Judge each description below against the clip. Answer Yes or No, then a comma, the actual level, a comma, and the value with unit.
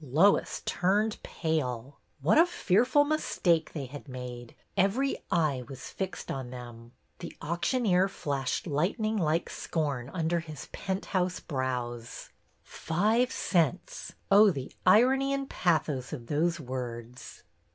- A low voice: No, medium, 165 Hz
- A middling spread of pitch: No, wide, 7.0 semitones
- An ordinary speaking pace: No, slow, 130 wpm